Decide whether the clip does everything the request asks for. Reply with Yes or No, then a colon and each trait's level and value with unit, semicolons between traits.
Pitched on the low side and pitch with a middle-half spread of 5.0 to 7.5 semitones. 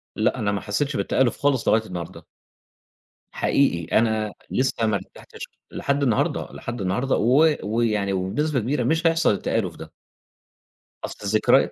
Yes: low, 115 Hz; average, 5.3 semitones